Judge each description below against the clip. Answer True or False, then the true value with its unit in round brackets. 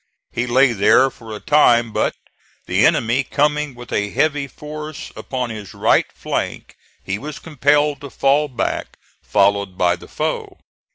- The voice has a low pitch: True (130 Hz)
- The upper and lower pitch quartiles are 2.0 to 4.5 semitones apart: False (5.1 semitones)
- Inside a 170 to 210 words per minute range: False (155 wpm)